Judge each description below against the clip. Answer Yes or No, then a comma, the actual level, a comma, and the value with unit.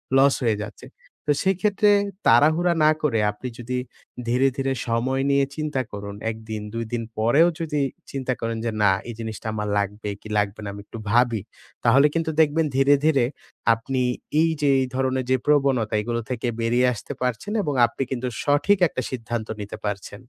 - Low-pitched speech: Yes, low, 125 Hz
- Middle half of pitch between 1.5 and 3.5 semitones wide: No, average, 4.2 semitones